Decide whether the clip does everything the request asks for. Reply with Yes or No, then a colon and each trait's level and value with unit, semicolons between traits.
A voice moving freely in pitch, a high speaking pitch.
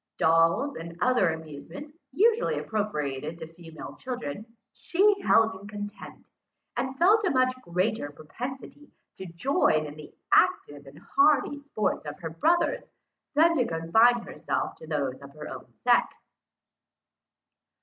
Yes: wide, 9.0 semitones; high, 200 Hz